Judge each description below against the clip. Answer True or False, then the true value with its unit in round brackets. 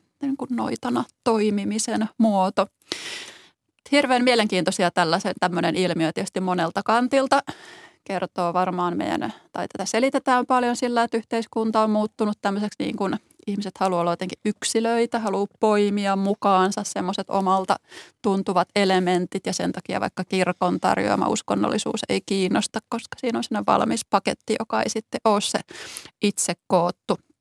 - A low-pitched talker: False (205 Hz)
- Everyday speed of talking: True (135 wpm)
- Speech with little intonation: False (3.7 semitones)